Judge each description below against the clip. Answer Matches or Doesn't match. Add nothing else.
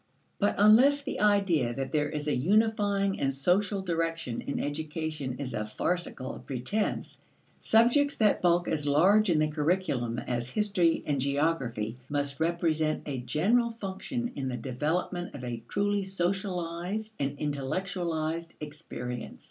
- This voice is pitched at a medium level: Matches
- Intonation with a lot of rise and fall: Matches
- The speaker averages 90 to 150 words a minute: Matches